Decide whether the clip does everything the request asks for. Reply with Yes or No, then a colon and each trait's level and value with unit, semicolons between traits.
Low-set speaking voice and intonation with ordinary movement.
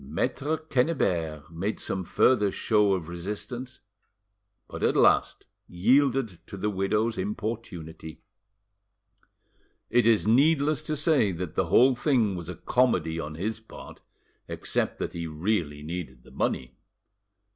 No: low, 105 Hz; wide, 6.5 semitones